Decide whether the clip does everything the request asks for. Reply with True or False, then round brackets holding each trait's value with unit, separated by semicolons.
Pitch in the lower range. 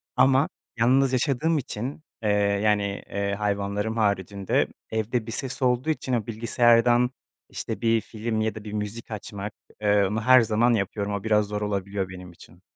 True (110 Hz)